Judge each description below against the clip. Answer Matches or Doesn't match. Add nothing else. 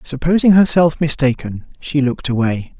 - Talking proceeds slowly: Matches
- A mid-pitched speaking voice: Matches